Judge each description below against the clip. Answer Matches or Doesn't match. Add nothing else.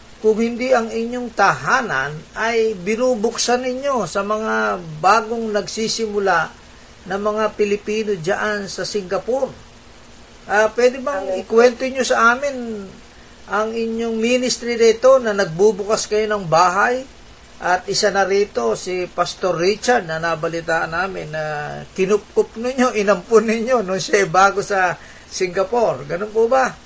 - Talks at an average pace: Matches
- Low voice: Doesn't match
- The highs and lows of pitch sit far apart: Doesn't match